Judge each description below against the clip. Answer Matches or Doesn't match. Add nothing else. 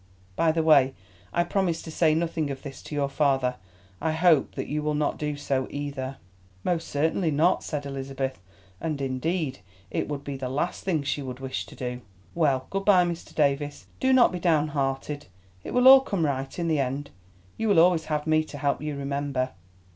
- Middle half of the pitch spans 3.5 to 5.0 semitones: Doesn't match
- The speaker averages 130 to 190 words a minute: Doesn't match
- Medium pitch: Matches